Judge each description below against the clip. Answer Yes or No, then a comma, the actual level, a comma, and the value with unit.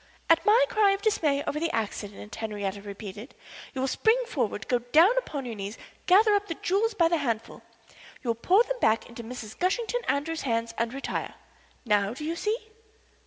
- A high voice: Yes, very high, 280 Hz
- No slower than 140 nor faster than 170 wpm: No, average, 195 wpm